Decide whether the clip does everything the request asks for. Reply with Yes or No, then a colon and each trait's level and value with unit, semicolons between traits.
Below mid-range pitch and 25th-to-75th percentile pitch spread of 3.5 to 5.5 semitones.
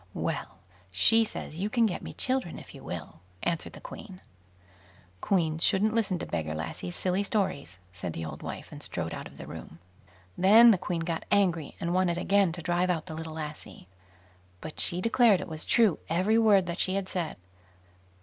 No: medium, 180 Hz; average, 4.2 semitones